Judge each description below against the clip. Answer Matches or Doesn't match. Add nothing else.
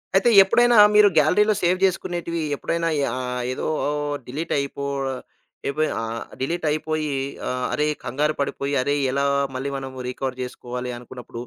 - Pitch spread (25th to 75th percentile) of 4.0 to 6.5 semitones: Matches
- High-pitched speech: Doesn't match